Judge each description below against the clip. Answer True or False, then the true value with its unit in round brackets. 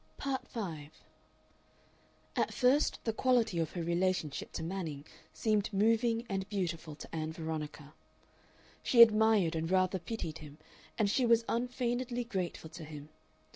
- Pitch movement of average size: False (6.3 semitones)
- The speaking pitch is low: False (190 Hz)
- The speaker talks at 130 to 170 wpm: True (135 wpm)